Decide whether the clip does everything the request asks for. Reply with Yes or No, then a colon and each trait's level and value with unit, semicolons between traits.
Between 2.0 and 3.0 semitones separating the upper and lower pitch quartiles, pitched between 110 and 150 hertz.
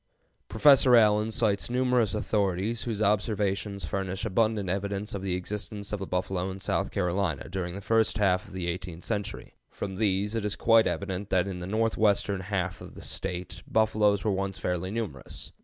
No: narrow, 2.5 semitones; low, 100 Hz